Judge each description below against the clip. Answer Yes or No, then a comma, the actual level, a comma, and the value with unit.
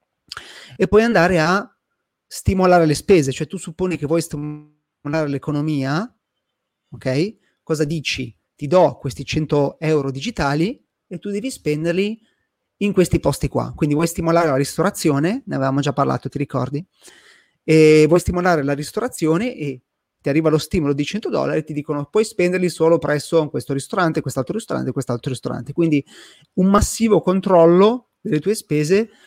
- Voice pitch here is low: No, medium, 160 Hz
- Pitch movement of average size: Yes, average, 4.0 semitones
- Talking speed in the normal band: Yes, average, 155 wpm